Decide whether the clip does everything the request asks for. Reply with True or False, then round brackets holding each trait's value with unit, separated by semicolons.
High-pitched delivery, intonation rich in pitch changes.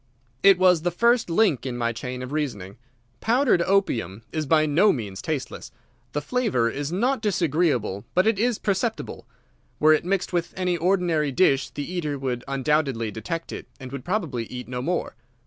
False (155 Hz; 6.6 semitones)